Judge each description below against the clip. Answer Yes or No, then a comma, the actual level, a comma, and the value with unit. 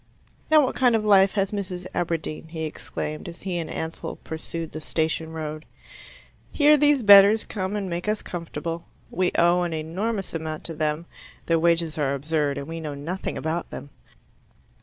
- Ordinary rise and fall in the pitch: Yes, average, 3.6 semitones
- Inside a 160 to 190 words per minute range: Yes, average, 180 wpm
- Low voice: No, medium, 170 Hz